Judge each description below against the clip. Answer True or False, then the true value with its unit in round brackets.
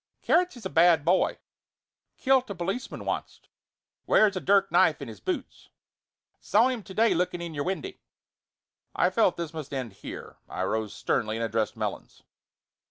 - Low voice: False (175 Hz)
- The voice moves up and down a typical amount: False (7.3 semitones)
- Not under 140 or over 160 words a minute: False (170 wpm)